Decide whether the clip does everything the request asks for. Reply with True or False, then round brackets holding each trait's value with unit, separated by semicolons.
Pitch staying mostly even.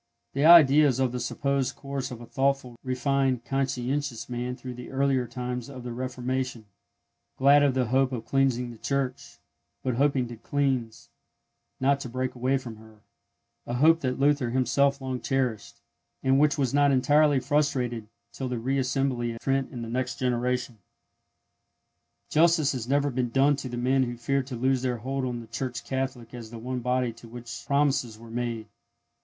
True (2.2 semitones)